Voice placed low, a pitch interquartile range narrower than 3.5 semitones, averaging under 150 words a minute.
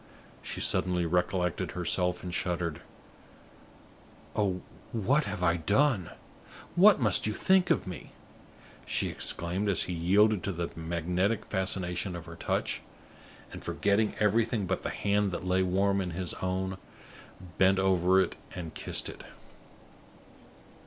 Yes: very low, 95 Hz; narrow, 2.4 semitones; slow, 135 wpm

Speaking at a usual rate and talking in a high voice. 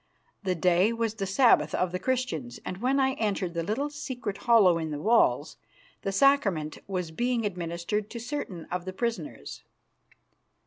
Yes: average, 165 wpm; high, 200 Hz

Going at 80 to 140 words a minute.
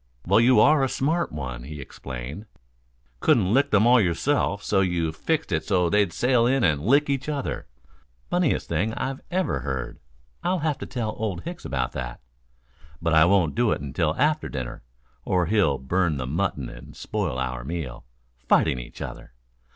No: average, 175 wpm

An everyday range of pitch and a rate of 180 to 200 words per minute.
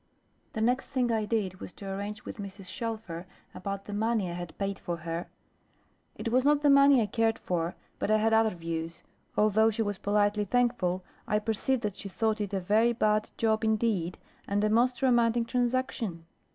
Yes: average, 3.0 semitones; average, 190 wpm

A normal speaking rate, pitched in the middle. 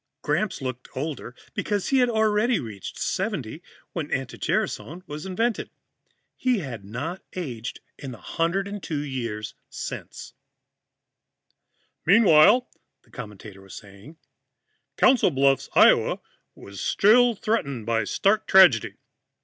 No: slow, 115 wpm; medium, 155 Hz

